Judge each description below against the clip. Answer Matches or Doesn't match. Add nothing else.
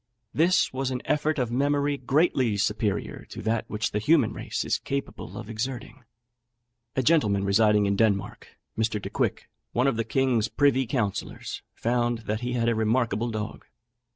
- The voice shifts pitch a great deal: Doesn't match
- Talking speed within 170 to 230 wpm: Doesn't match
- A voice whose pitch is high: Doesn't match